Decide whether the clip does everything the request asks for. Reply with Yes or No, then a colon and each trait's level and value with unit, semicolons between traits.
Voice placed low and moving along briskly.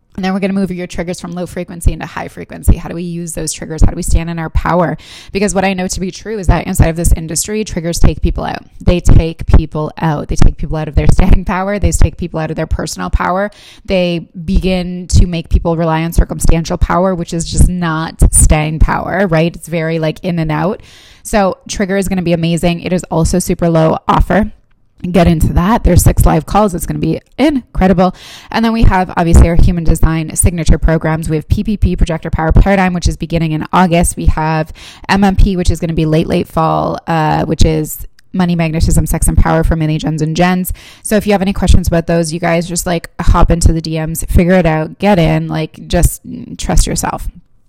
No: medium, 170 Hz; fast, 225 wpm